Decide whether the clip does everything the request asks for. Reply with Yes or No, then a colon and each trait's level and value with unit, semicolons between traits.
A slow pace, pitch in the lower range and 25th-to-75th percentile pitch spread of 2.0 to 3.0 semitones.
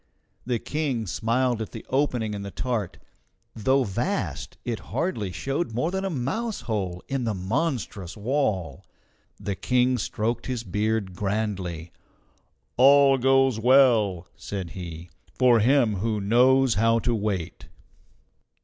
No: slow, 130 wpm; low, 115 Hz; average, 4.7 semitones